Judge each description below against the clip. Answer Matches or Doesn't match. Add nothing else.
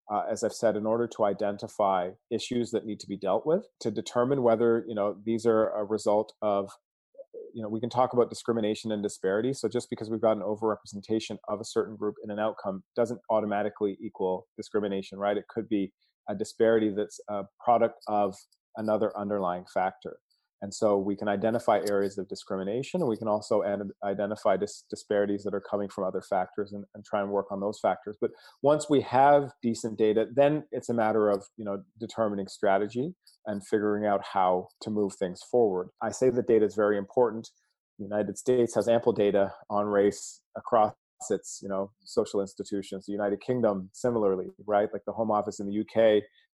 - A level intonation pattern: Matches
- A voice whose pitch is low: Matches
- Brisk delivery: Doesn't match